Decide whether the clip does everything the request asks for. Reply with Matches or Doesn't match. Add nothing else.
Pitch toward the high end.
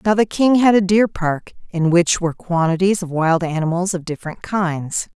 Doesn't match